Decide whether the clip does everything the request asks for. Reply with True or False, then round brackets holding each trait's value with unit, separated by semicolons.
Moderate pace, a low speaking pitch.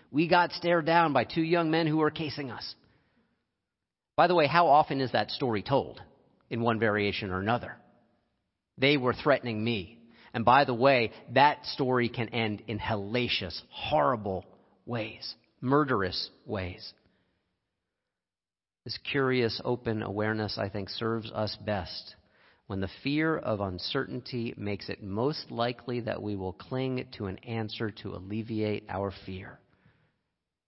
True (145 wpm; 115 Hz)